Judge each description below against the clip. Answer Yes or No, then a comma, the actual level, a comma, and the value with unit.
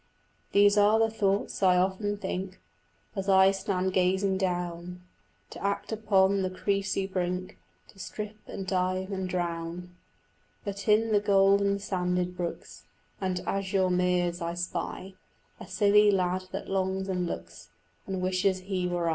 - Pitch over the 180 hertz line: Yes, high, 190 Hz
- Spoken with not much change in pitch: Yes, narrow, 1.7 semitones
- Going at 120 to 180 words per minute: Yes, average, 145 wpm